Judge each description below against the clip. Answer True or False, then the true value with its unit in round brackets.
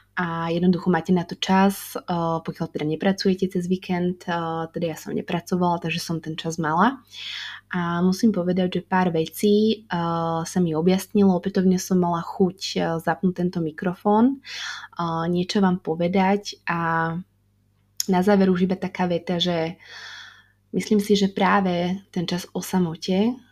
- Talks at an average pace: True (140 wpm)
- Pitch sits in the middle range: True (180 Hz)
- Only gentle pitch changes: True (2.3 semitones)